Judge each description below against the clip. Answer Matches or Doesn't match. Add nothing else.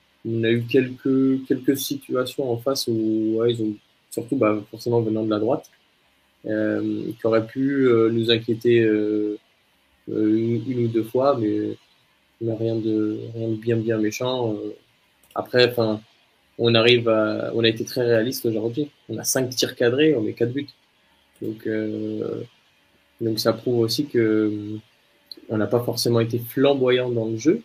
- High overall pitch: Doesn't match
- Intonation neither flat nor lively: Doesn't match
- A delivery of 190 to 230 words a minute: Doesn't match